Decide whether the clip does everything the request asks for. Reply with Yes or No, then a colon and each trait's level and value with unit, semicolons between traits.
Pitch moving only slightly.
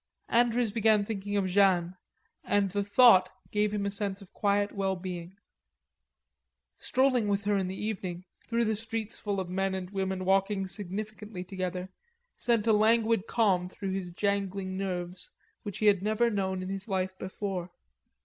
Yes: narrow, 2.1 semitones